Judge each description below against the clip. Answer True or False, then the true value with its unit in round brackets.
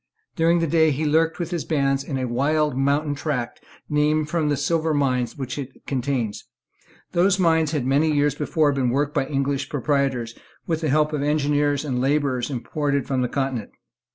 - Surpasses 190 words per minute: False (180 wpm)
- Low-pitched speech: False (145 Hz)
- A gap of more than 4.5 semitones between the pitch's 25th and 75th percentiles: False (2.4 semitones)